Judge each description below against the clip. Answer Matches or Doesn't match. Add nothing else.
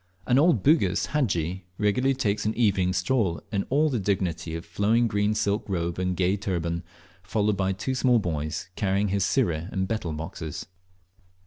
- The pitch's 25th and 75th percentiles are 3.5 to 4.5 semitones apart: Matches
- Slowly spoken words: Doesn't match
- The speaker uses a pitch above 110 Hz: Doesn't match